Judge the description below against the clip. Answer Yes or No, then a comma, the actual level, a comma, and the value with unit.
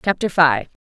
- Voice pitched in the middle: Yes, medium, 160 Hz